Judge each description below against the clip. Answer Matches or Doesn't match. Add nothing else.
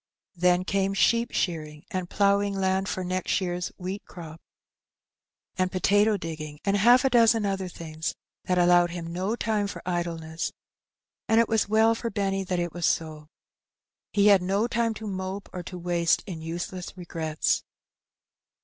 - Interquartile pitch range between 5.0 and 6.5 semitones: Doesn't match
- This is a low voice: Doesn't match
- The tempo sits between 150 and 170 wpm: Matches